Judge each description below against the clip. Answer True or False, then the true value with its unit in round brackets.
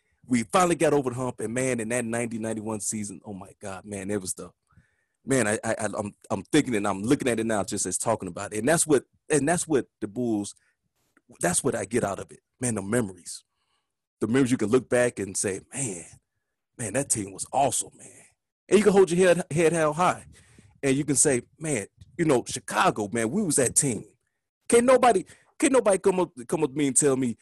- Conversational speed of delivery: False (230 wpm)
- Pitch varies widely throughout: True (6.2 semitones)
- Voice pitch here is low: True (120 Hz)